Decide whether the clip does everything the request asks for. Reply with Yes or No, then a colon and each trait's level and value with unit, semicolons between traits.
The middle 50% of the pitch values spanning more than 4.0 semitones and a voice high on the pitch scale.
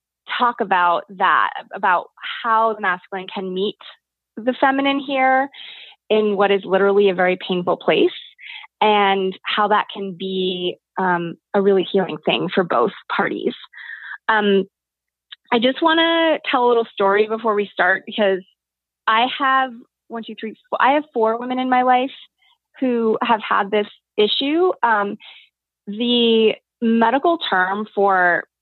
Yes: average, 4.5 semitones; high, 220 Hz